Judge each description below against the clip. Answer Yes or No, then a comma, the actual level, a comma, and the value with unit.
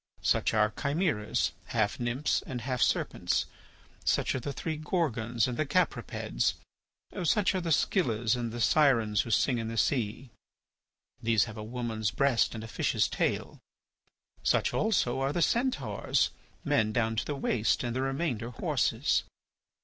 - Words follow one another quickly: No, average, 150 wpm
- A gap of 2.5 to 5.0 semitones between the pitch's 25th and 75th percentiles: Yes, average, 4.4 semitones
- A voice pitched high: No, low, 120 Hz